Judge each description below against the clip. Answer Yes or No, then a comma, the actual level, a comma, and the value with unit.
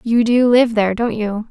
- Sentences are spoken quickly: Yes, fast, 240 wpm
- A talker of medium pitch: No, high, 225 Hz